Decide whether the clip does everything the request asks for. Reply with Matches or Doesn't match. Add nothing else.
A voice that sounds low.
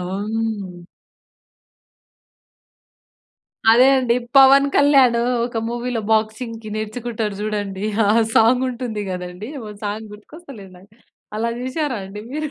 Doesn't match